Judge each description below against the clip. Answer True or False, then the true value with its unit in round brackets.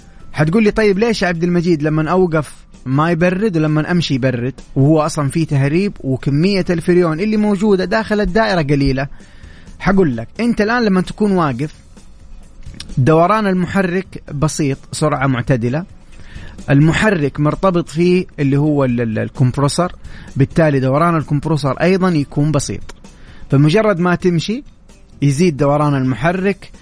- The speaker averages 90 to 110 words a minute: False (125 wpm)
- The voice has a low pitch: False (155 Hz)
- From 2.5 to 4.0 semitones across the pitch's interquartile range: False (4.9 semitones)